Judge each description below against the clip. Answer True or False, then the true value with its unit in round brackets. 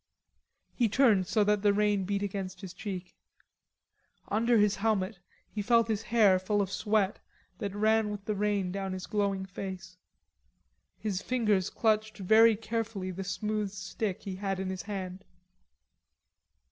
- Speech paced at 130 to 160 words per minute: True (150 wpm)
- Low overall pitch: False (205 Hz)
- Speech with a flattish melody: True (2.1 semitones)